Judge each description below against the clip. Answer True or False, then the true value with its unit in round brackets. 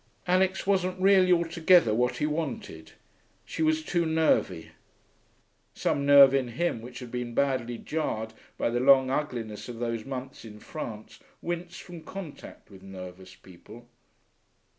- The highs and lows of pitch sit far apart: True (6.3 semitones)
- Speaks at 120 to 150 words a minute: True (140 wpm)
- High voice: False (135 Hz)